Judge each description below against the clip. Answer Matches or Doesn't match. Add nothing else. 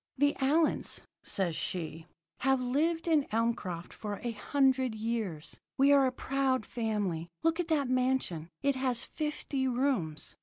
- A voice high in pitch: Matches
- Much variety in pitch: Doesn't match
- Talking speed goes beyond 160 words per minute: Doesn't match